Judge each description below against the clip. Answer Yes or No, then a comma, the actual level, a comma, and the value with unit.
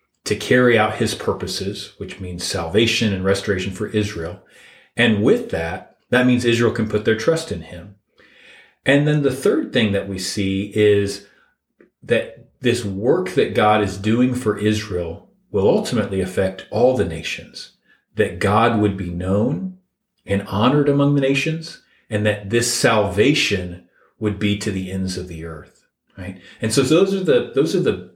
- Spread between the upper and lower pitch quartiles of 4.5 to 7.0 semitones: No, average, 4.0 semitones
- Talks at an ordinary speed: Yes, average, 170 wpm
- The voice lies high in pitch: No, low, 105 Hz